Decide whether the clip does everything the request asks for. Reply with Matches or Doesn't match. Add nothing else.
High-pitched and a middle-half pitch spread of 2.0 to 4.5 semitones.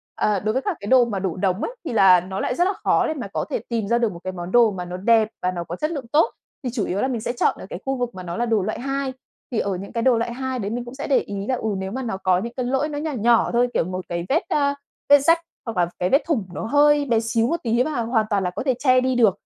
Doesn't match